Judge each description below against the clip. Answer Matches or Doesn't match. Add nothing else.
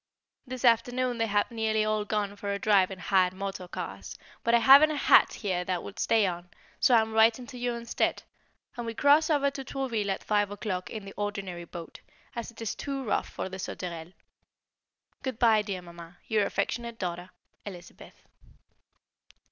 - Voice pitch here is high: Matches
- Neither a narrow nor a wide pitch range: Matches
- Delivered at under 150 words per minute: Doesn't match